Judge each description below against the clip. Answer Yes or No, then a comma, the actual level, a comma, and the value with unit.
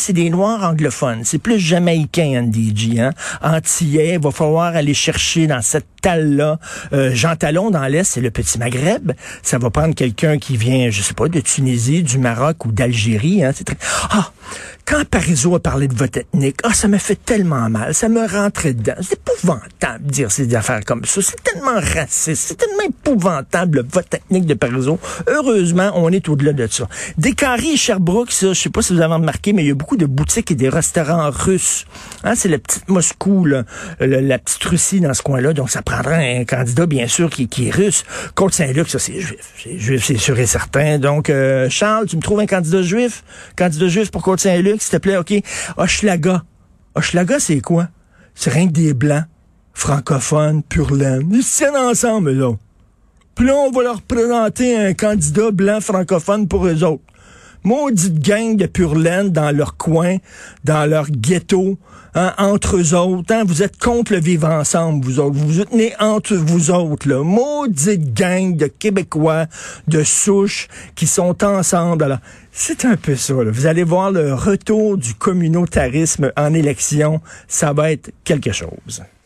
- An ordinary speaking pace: Yes, average, 190 wpm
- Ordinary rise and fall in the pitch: No, wide, 5.8 semitones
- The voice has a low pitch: No, medium, 165 Hz